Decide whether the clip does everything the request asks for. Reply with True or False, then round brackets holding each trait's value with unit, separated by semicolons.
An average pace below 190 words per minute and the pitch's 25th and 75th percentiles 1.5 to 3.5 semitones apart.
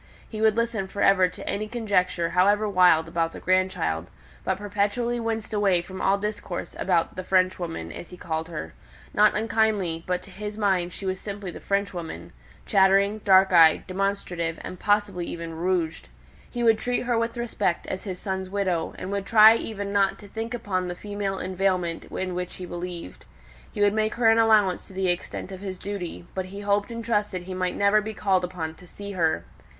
False (195 wpm; 2.5 semitones)